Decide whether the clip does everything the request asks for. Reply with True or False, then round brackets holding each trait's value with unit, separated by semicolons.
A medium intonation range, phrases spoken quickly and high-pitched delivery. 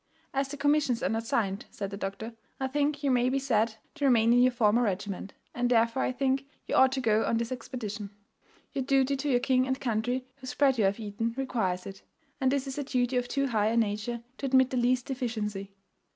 True (3.2 semitones; 225 wpm; 245 Hz)